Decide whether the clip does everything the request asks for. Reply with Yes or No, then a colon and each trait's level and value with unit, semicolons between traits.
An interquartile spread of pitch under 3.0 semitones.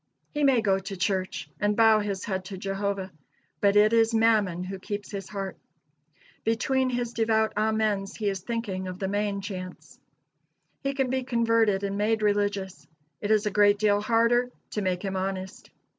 Yes: narrow, 2.5 semitones